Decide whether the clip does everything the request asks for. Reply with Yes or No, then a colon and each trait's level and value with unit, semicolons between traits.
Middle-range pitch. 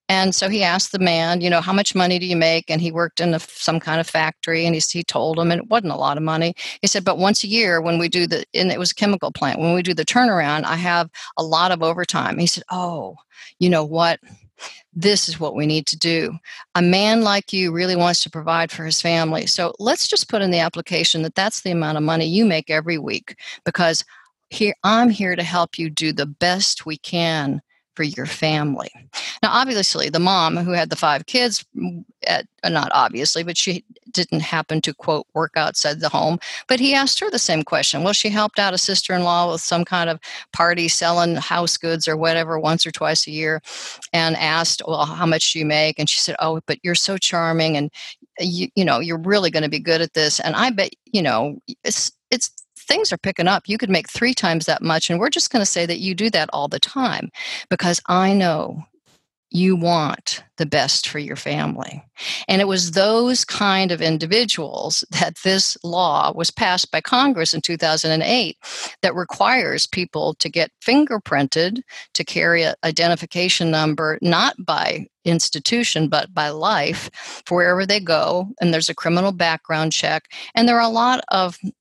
Yes: medium, 170 Hz